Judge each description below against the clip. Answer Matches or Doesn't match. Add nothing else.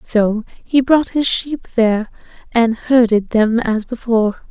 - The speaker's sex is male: Doesn't match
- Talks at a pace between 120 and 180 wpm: Matches